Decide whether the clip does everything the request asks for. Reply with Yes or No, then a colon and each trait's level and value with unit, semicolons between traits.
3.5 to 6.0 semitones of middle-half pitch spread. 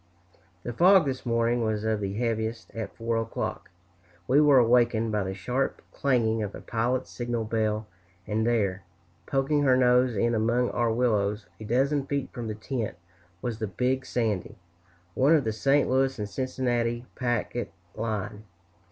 No: average, 2.7 semitones